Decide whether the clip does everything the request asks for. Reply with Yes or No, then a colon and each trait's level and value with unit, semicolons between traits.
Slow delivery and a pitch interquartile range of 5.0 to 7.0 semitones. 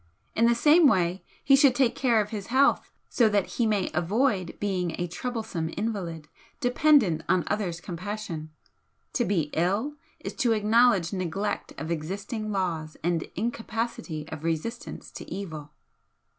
No: average, 145 wpm; wide, 5.4 semitones